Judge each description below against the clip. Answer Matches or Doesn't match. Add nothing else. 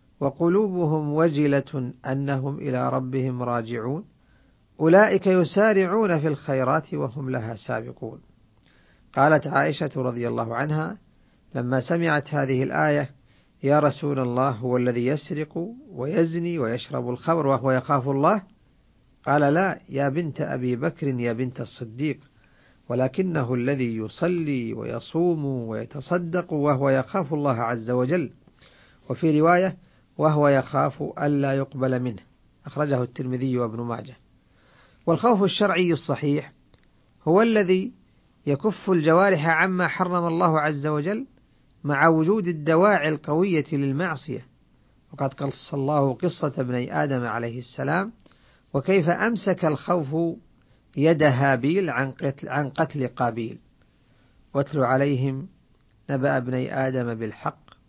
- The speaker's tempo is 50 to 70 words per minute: Doesn't match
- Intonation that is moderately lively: Matches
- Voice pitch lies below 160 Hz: Matches